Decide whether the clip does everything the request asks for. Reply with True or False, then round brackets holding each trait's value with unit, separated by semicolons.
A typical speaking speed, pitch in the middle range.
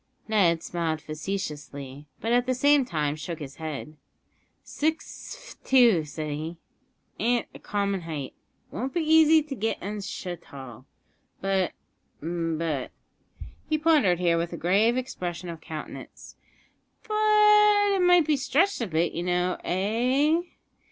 False (145 wpm; 195 Hz)